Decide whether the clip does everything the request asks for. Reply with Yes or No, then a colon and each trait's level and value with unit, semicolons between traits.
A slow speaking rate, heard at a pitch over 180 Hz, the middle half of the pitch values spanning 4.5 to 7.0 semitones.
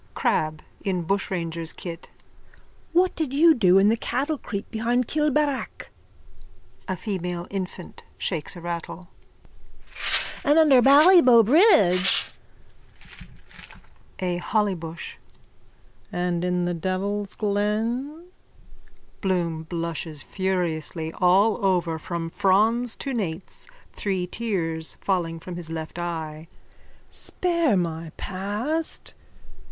Yes: slow, 100 wpm; high, 190 Hz; wide, 5.5 semitones